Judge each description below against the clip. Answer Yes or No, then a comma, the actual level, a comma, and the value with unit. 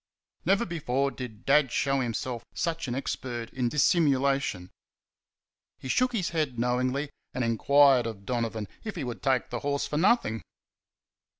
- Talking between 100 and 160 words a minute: Yes, average, 145 wpm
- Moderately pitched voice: No, low, 130 Hz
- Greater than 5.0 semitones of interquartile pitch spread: No, average, 3.7 semitones